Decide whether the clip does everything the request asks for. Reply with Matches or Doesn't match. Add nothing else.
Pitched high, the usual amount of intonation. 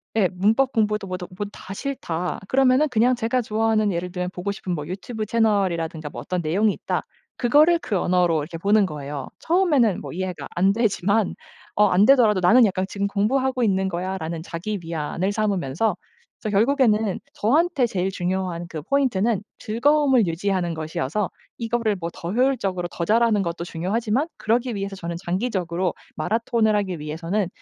Matches